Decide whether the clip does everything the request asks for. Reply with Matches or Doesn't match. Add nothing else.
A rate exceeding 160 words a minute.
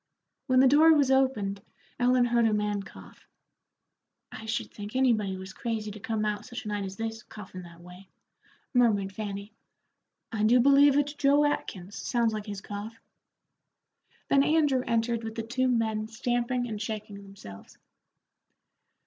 Doesn't match